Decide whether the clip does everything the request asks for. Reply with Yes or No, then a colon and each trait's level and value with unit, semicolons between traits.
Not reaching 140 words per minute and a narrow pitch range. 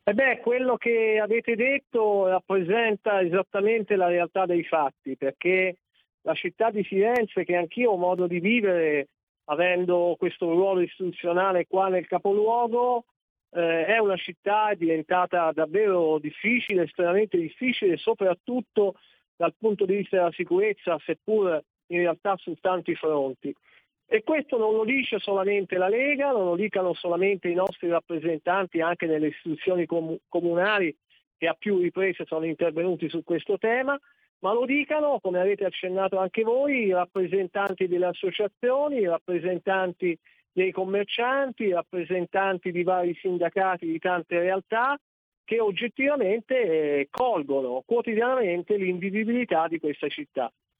No: average, 130 wpm; average, 4.1 semitones